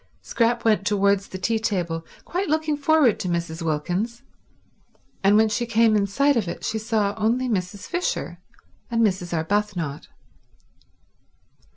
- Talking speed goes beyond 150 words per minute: No, average, 145 wpm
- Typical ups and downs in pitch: Yes, average, 4.2 semitones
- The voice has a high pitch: Yes, high, 210 Hz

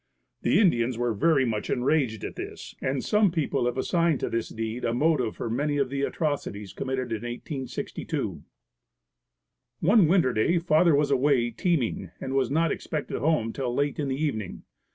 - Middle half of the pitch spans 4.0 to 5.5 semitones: Yes, average, 4.6 semitones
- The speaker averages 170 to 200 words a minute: Yes, average, 175 wpm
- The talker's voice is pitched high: No, low, 135 Hz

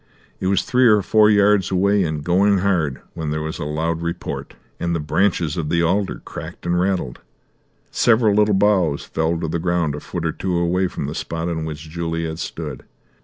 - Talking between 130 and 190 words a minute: No, average, 200 wpm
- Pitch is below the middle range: Yes, very low, 85 Hz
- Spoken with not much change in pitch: No, average, 3.5 semitones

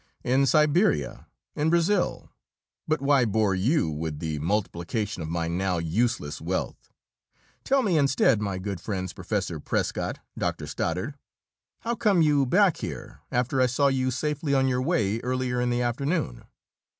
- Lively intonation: Yes, wide, 7.4 semitones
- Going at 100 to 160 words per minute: Yes, average, 150 wpm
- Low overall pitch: Yes, low, 125 Hz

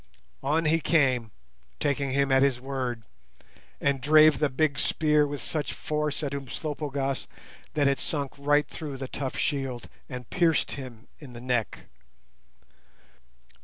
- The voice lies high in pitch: No, medium, 140 Hz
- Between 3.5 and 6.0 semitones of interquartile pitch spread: No, narrow, 2.4 semitones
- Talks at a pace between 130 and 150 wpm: Yes, average, 140 wpm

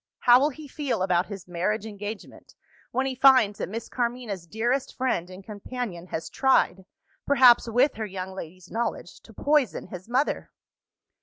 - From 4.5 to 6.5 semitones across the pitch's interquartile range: Yes, wide, 5.4 semitones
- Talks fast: No, average, 160 wpm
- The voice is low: No, high, 220 Hz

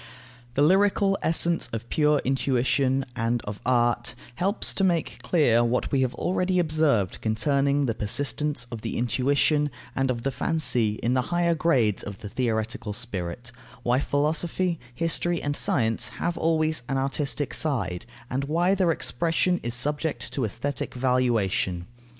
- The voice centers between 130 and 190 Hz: Yes, low, 135 Hz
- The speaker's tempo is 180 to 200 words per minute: No, average, 150 wpm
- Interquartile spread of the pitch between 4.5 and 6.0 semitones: Yes, average, 5.0 semitones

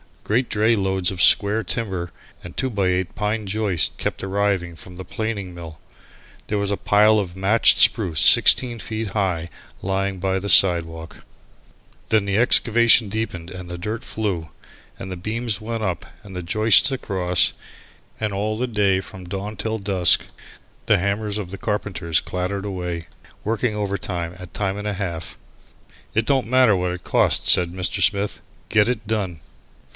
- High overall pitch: No, low, 100 Hz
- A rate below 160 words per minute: No, average, 165 wpm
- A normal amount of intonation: Yes, average, 3.0 semitones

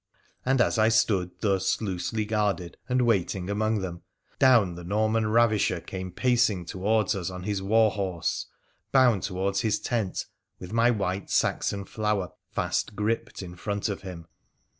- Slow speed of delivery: No, average, 155 wpm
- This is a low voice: Yes, low, 100 Hz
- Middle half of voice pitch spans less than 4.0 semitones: Yes, average, 3.0 semitones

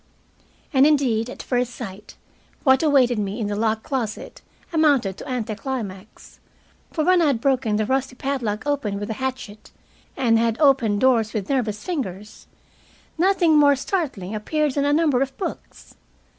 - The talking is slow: No, average, 160 wpm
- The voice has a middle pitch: No, very high, 250 Hz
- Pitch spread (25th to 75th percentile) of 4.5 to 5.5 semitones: Yes, average, 4.8 semitones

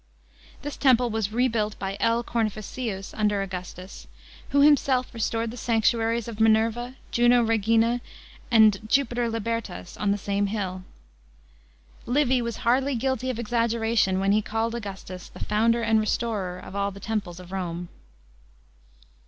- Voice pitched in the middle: No, high, 225 Hz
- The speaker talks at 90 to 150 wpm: Yes, average, 140 wpm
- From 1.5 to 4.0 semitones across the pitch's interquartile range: Yes, average, 2.9 semitones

